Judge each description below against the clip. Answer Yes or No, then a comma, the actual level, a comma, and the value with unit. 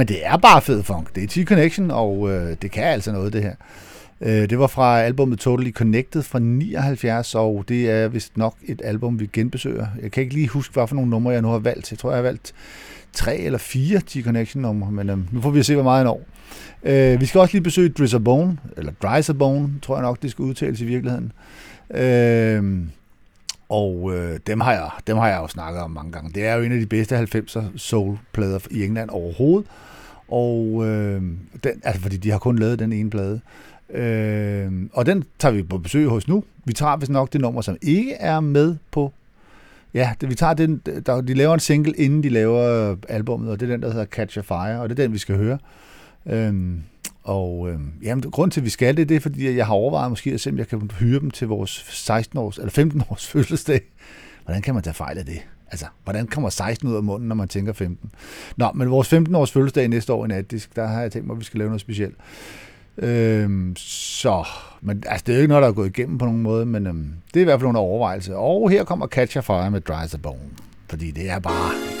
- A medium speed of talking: No, fast, 235 wpm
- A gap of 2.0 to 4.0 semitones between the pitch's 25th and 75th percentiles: No, average, 4.8 semitones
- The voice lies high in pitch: No, low, 115 Hz